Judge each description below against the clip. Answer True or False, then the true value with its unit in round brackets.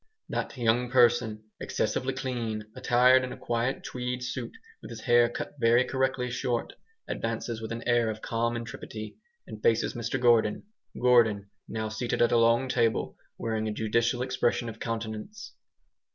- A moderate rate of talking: True (155 wpm)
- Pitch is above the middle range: False (120 Hz)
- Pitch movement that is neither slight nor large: False (1.8 semitones)